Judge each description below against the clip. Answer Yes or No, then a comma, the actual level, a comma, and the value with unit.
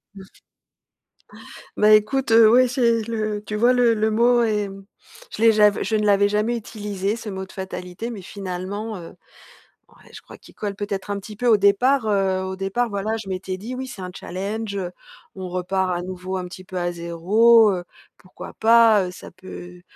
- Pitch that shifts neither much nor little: Yes, average, 3.0 semitones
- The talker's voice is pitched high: Yes, high, 205 Hz